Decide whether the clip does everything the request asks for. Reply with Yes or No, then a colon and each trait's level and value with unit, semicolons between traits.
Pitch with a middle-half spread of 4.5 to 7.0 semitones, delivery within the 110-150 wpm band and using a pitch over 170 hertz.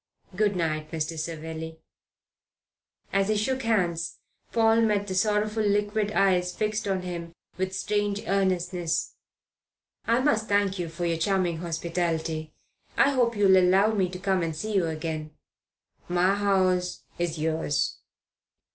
No: average, 3.7 semitones; average, 140 wpm; medium, 185 Hz